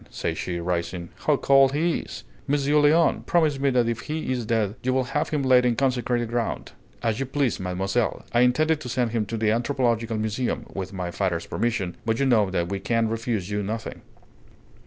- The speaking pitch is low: Yes, low, 120 Hz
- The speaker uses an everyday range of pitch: Yes, average, 4.3 semitones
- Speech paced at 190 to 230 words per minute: Yes, average, 200 wpm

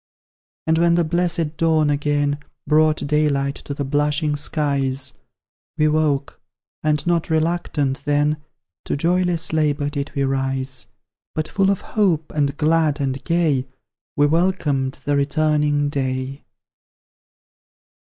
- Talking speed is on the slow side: Yes, slow, 125 wpm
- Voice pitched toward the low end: No, medium, 150 Hz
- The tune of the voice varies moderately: No, narrow, 2.2 semitones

